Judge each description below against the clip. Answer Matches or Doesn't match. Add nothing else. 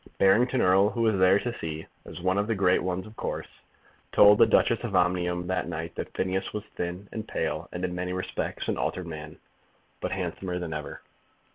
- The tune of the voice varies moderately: Doesn't match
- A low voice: Matches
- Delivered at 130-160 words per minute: Doesn't match